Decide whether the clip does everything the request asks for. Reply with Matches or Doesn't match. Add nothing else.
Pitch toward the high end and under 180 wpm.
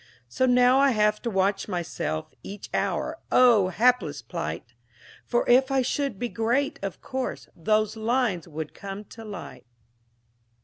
Matches